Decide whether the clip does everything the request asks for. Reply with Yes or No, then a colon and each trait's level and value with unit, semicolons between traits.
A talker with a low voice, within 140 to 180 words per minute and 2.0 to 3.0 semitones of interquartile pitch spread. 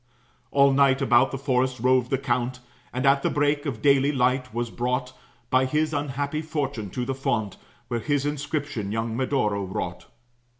Yes: low, 130 Hz; average, 170 wpm; narrow, 2.6 semitones